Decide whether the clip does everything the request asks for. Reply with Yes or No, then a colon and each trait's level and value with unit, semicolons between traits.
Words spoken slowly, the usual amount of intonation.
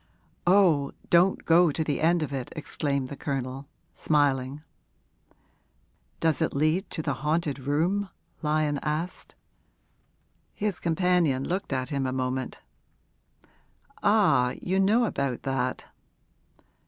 Yes: slow, 115 wpm; average, 4.2 semitones